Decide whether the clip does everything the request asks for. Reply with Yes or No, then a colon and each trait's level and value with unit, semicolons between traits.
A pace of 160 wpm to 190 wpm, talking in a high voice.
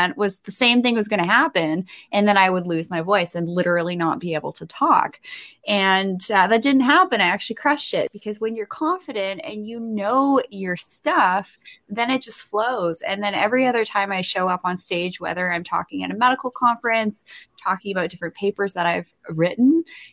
No: fast, 205 wpm; high, 205 Hz